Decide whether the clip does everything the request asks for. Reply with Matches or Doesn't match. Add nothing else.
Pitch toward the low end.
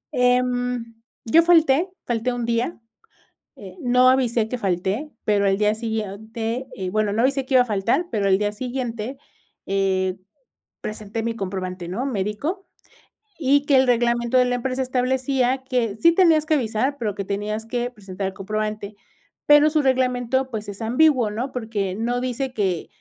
Doesn't match